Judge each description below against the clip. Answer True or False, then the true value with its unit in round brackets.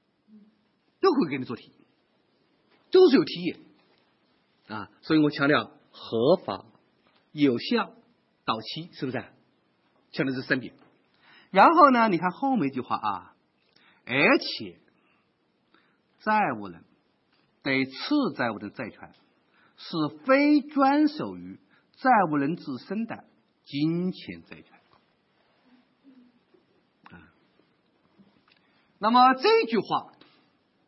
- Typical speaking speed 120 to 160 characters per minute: True (145 characters per minute)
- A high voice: True (200 Hz)